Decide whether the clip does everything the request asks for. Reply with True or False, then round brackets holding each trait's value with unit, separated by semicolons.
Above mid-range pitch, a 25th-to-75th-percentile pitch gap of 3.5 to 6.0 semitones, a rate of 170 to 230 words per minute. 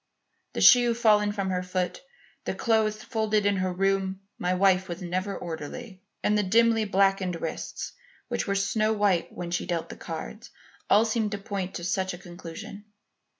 False (195 Hz; 2.7 semitones; 180 wpm)